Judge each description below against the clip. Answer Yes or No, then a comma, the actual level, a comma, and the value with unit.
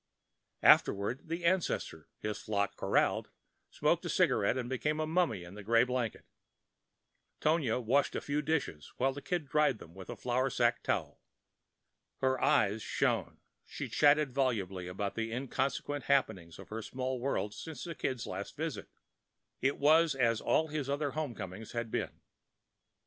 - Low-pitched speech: Yes, low, 130 Hz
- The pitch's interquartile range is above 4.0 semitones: Yes, average, 5.0 semitones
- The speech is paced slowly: No, average, 160 wpm